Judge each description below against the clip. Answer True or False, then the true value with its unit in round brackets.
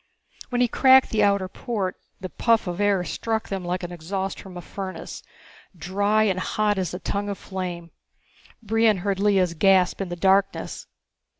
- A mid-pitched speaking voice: False (195 Hz)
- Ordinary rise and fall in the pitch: False (2.2 semitones)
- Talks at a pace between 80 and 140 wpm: False (175 wpm)